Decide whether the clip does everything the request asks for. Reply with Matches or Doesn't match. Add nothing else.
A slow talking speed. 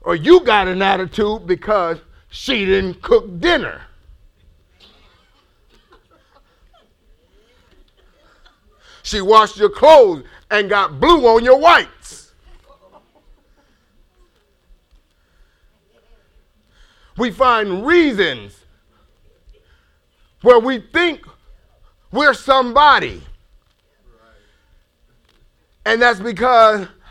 Matches